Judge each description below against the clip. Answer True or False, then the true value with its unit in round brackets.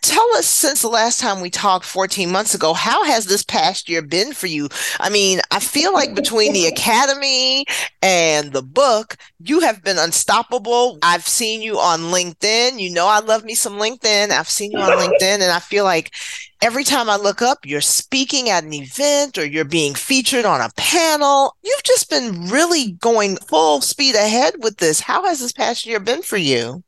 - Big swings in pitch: True (6.6 semitones)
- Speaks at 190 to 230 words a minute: True (200 wpm)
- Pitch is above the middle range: True (210 Hz)